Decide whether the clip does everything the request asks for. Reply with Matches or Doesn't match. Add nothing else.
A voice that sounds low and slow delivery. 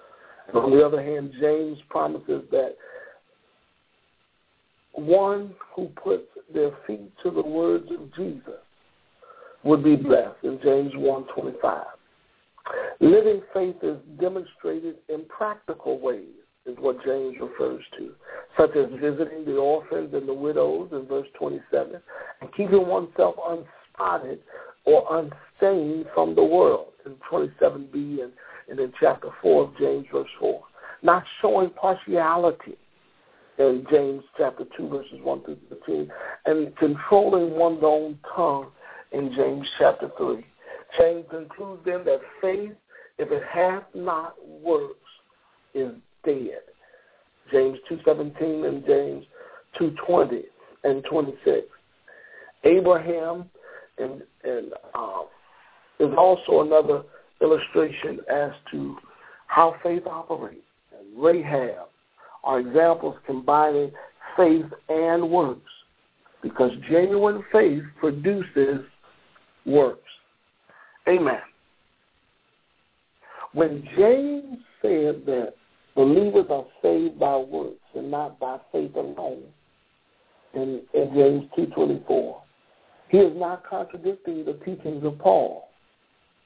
Doesn't match